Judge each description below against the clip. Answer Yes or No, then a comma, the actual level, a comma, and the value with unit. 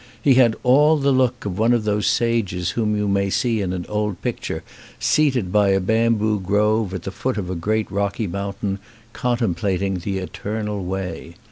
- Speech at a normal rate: Yes, average, 180 wpm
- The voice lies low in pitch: Yes, low, 105 Hz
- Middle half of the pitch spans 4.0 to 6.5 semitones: No, average, 3.1 semitones